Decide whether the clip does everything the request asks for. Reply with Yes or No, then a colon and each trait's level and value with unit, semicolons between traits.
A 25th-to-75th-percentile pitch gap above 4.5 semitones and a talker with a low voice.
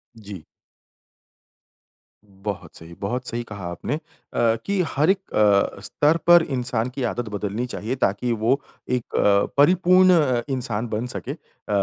Yes: wide, 5.6 semitones; low, 120 Hz